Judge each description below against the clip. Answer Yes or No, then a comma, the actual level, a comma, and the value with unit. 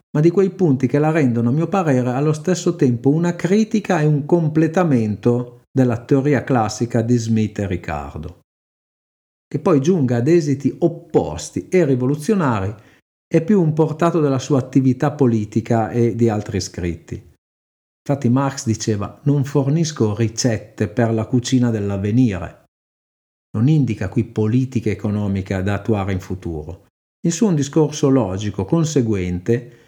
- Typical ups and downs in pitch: No, wide, 5.9 semitones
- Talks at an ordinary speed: Yes, average, 140 wpm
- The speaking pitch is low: Yes, low, 125 Hz